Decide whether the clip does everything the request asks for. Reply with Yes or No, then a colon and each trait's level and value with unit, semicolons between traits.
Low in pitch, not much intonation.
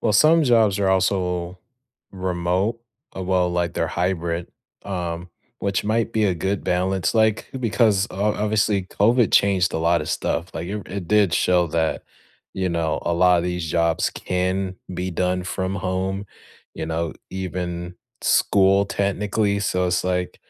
Yes: very low, 95 Hz; narrow, 2.3 semitones